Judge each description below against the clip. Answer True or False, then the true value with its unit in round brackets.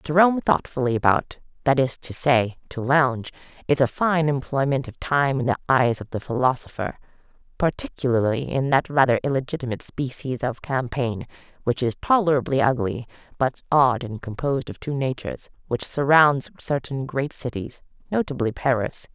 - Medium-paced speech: True (150 wpm)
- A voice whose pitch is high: False (135 Hz)